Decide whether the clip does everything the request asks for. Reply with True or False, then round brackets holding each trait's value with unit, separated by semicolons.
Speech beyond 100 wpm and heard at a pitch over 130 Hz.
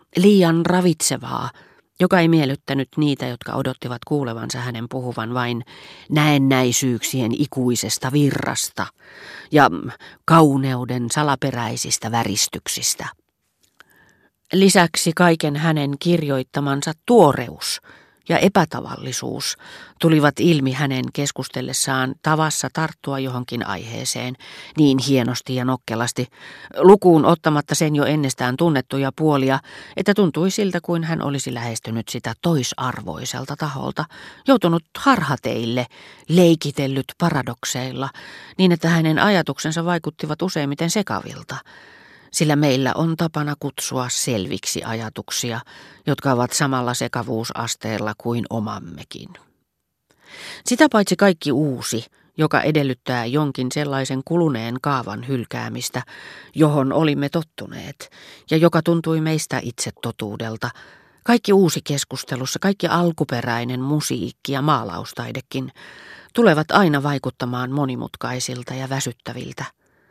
False (95 wpm; 140 Hz)